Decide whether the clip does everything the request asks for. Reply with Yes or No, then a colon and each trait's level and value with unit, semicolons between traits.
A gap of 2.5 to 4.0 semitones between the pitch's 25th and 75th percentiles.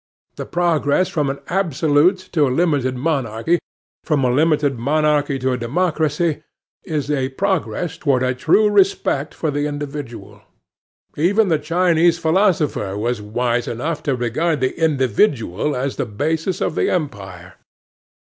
No: average, 4.5 semitones